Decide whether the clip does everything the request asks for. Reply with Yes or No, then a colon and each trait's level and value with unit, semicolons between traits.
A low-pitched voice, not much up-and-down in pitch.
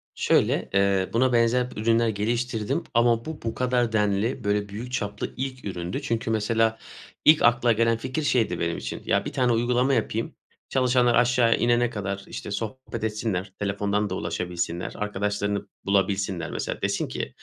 No: low, 115 Hz; average, 3.1 semitones